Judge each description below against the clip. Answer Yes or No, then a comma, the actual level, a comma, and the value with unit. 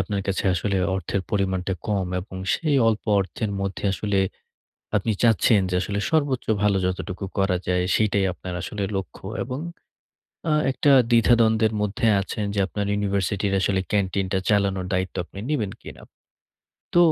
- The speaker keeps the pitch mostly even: Yes, narrow, 2.3 semitones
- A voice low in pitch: Yes, low, 100 Hz